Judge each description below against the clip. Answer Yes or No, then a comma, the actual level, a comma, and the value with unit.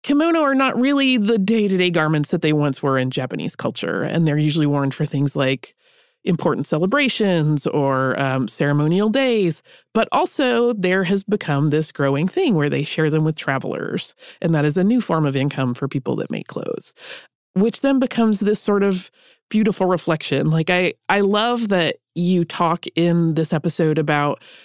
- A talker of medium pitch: Yes, medium, 170 Hz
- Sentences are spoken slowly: No, average, 180 wpm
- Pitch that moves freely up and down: Yes, wide, 6.3 semitones